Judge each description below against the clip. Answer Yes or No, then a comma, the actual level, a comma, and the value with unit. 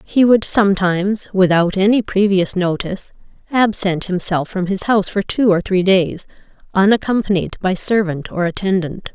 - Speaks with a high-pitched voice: Yes, high, 195 Hz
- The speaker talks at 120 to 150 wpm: Yes, average, 145 wpm